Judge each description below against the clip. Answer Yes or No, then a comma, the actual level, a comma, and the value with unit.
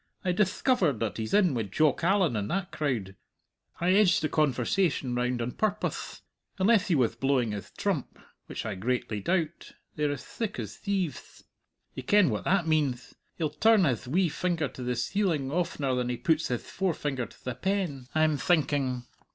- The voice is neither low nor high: Yes, medium, 150 Hz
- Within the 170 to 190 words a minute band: Yes, average, 175 wpm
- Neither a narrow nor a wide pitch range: No, wide, 6.6 semitones